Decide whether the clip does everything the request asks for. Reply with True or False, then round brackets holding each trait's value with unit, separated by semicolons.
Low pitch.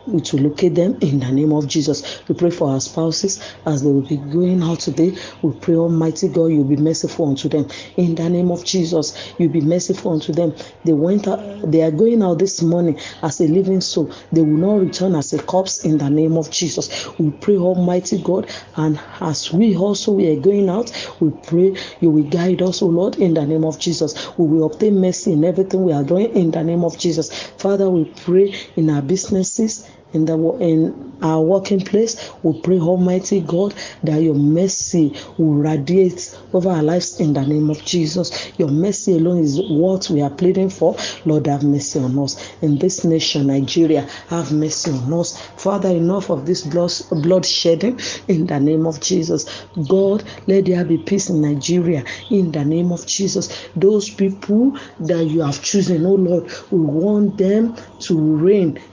False (170 Hz)